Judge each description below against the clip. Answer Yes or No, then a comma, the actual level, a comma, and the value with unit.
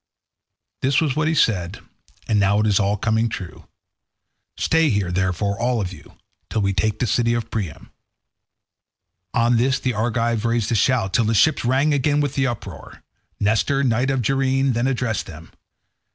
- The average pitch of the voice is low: Yes, low, 115 Hz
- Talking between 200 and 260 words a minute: No, average, 175 wpm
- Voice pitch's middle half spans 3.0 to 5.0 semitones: Yes, average, 4.3 semitones